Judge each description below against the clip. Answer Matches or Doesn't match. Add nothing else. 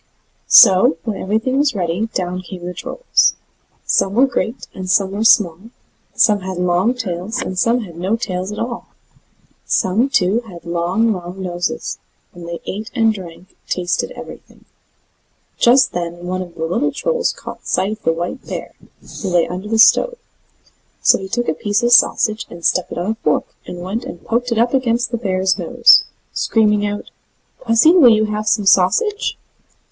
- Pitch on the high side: Matches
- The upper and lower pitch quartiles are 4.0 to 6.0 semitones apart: Matches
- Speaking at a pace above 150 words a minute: Matches